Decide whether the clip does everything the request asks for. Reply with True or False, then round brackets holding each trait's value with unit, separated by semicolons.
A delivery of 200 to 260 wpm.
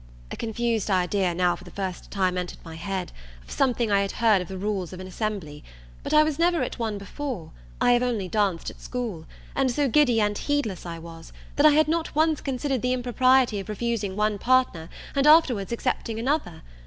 True (205 wpm)